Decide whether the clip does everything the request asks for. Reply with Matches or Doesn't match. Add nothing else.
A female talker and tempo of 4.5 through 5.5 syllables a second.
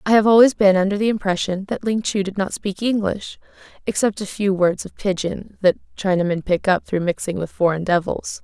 Matches